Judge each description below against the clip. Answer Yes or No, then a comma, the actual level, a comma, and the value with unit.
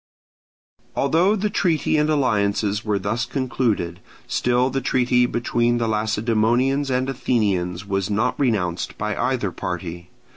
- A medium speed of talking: No, slow, 125 wpm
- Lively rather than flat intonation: No, average, 4.3 semitones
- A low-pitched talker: Yes, low, 120 Hz